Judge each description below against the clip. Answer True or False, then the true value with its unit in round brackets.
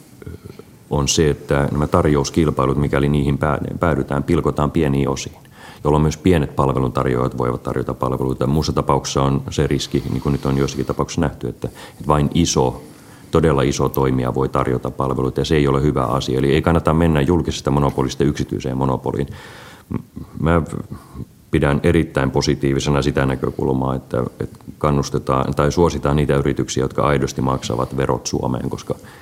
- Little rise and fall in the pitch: True (2.0 semitones)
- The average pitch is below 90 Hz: True (70 Hz)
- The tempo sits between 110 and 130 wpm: False (150 wpm)